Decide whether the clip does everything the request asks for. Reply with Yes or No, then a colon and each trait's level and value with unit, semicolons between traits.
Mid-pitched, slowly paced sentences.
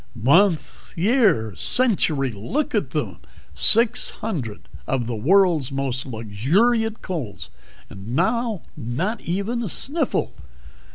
Yes: medium, 165 Hz; slow, 110 wpm